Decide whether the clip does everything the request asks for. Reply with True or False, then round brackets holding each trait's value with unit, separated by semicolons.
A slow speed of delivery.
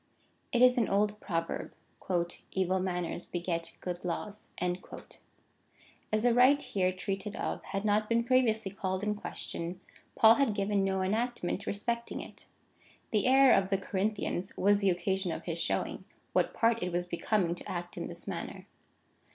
False (160 wpm)